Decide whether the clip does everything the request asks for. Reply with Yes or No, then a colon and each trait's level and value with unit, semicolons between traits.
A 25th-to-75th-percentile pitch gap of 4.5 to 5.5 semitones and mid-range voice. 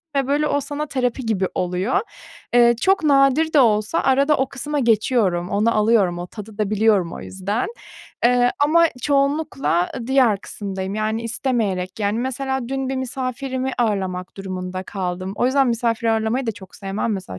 No: average, 5.2 semitones; high, 230 Hz